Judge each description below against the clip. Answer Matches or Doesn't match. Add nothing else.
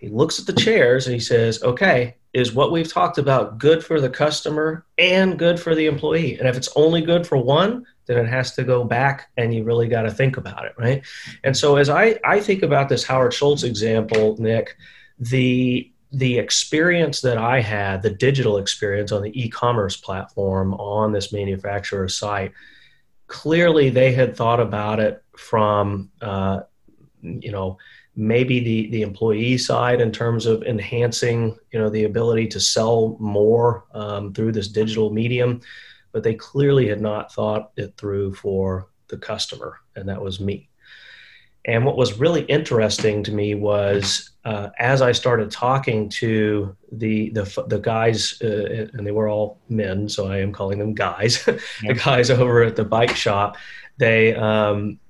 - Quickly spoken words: Doesn't match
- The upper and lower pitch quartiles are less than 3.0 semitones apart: Doesn't match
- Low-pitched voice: Matches